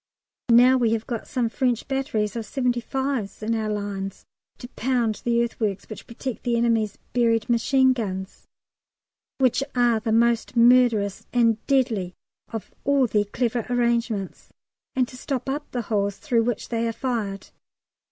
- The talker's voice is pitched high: Yes, high, 235 Hz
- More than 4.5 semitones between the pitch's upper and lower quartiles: No, narrow, 2.4 semitones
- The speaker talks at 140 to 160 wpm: Yes, average, 150 wpm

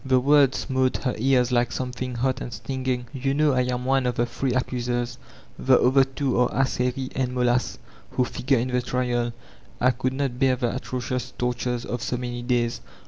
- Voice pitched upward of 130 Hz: No, low, 125 Hz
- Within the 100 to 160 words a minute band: No, average, 195 wpm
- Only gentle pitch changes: Yes, narrow, 1.2 semitones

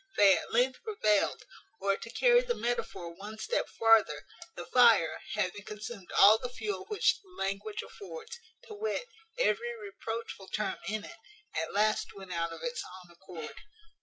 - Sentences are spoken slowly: No, average, 165 wpm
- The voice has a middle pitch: No, high, 215 Hz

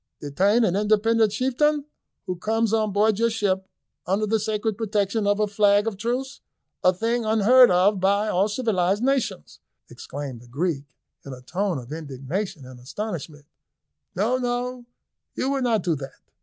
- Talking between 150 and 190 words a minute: Yes, average, 160 wpm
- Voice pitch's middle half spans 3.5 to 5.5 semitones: Yes, average, 4.0 semitones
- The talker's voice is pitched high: Yes, high, 205 Hz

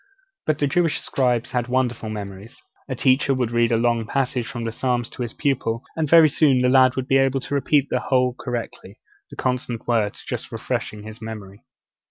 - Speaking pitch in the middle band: No, low, 125 Hz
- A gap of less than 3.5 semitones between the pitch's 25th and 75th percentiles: Yes, narrow, 2.6 semitones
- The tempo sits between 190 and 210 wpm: Yes, average, 200 wpm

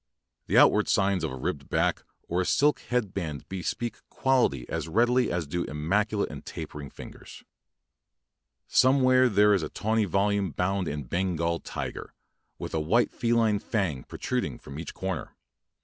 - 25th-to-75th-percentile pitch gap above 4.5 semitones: Yes, wide, 5.6 semitones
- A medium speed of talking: Yes, average, 155 wpm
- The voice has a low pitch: Yes, very low, 95 Hz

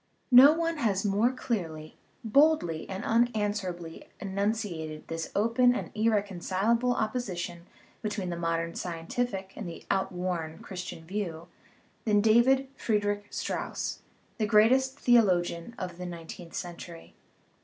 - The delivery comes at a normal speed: No, slow, 120 wpm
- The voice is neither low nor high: No, high, 200 Hz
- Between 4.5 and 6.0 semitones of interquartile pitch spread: Yes, average, 4.9 semitones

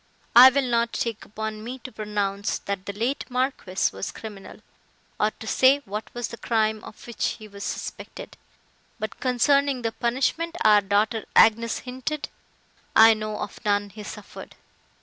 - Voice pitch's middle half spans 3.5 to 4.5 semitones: No, average, 3.1 semitones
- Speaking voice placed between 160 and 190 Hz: No, high, 220 Hz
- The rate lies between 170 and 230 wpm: No, average, 160 wpm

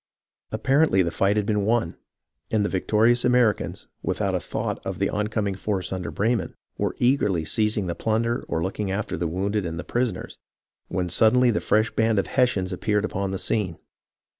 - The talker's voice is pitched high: No, low, 105 Hz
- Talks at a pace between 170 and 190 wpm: Yes, average, 180 wpm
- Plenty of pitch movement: No, average, 3.2 semitones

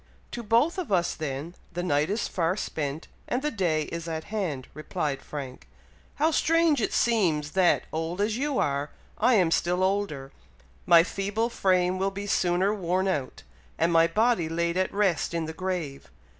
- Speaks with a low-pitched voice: No, medium, 180 Hz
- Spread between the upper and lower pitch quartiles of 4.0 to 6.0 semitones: Yes, average, 4.4 semitones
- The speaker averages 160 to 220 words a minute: Yes, average, 175 wpm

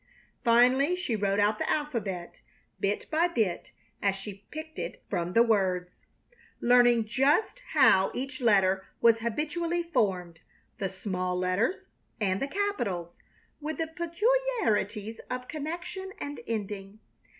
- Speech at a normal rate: No, slow, 130 wpm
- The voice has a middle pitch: No, high, 230 Hz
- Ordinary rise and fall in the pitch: No, wide, 8.1 semitones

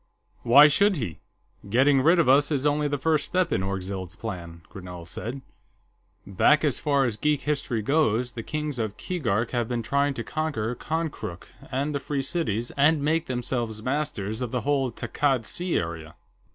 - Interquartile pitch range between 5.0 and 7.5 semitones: Yes, average, 5.3 semitones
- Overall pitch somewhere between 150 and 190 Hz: No, low, 130 Hz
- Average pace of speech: Yes, average, 175 wpm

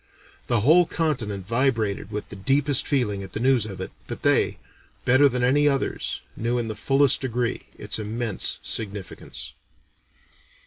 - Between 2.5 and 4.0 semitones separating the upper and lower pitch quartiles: No, average, 4.4 semitones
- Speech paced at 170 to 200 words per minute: No, average, 150 wpm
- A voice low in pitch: Yes, low, 120 Hz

